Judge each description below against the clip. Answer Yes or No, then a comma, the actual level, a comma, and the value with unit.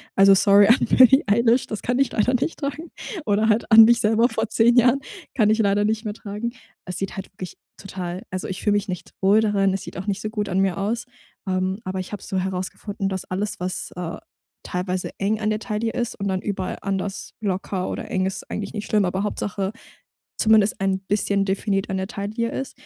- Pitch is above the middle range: Yes, high, 205 Hz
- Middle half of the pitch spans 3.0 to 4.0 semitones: No, narrow, 2.5 semitones